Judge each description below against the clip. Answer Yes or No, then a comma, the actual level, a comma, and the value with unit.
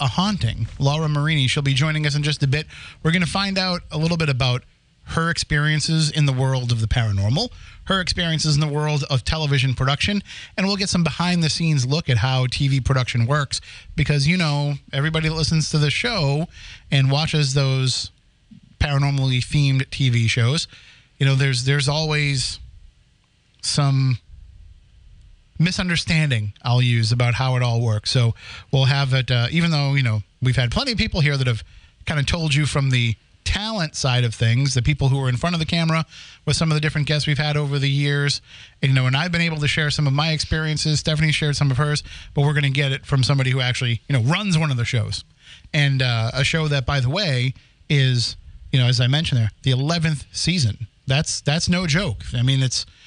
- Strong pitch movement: No, average, 3.7 semitones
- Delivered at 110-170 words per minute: No, fast, 205 wpm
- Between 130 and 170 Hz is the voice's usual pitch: Yes, medium, 140 Hz